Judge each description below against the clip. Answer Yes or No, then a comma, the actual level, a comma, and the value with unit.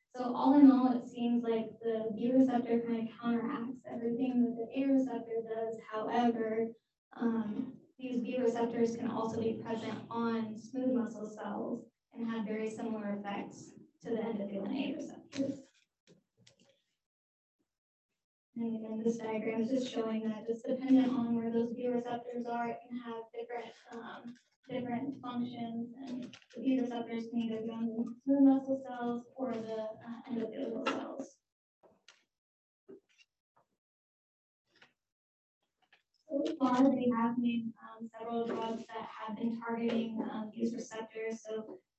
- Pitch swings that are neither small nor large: No, narrow, 1.8 semitones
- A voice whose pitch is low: No, high, 235 Hz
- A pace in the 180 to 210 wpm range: No, average, 140 wpm